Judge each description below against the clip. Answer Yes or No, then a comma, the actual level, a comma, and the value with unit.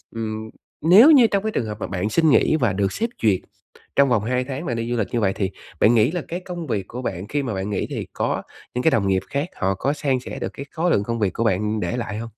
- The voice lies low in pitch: Yes, low, 115 Hz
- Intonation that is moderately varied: No, wide, 5.8 semitones